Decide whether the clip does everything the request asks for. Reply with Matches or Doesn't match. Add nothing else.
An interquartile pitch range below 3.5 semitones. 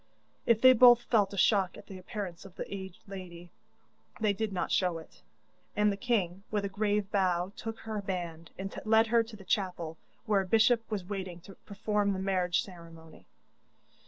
Matches